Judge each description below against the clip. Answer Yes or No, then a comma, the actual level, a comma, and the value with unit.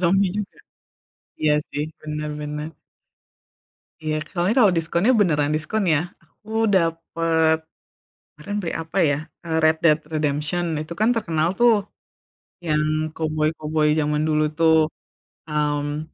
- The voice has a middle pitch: Yes, medium, 155 Hz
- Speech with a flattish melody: Yes, narrow, 2.1 semitones